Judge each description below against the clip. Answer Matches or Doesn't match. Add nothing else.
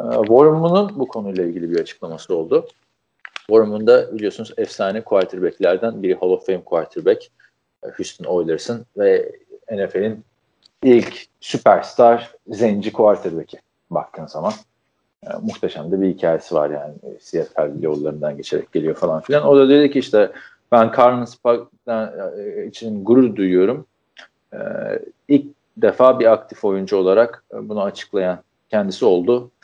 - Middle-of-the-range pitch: Doesn't match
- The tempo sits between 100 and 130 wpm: Matches